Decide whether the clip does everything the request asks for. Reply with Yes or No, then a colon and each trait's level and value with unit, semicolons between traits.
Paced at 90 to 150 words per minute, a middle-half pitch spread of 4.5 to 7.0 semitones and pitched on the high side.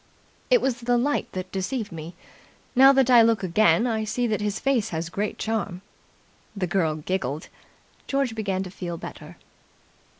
No: average, 165 wpm; average, 4.9 semitones; high, 210 Hz